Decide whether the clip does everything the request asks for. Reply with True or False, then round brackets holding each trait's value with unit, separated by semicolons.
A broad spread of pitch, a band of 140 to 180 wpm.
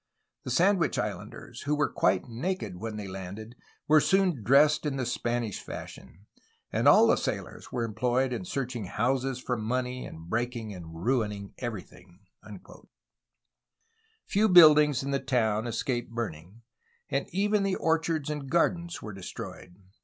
True (5.7 semitones; 145 wpm)